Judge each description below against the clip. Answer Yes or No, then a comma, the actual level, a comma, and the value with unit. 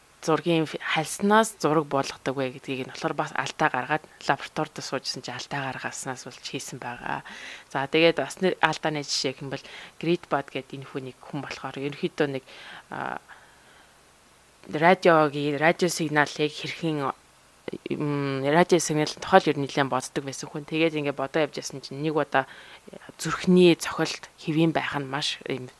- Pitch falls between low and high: Yes, medium, 150 Hz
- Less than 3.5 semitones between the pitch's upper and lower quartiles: Yes, average, 2.9 semitones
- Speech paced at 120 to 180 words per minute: Yes, average, 150 wpm